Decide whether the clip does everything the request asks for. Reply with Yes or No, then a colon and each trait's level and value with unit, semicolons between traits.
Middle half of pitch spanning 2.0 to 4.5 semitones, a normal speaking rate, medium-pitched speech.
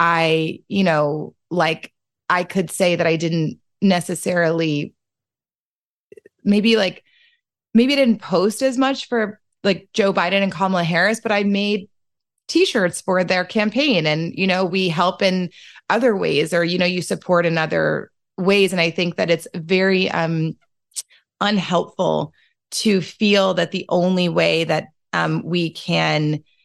Yes: average, 3.3 semitones; average, 150 wpm; medium, 180 Hz